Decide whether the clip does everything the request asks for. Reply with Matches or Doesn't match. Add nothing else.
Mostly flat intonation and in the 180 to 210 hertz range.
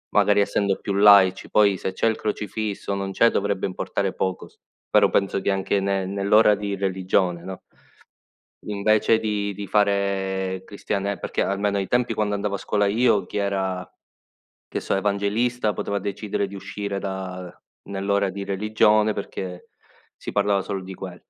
Doesn't match